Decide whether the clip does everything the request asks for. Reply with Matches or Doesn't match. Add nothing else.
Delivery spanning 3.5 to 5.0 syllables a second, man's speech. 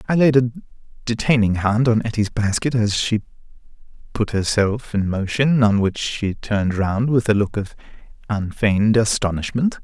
Matches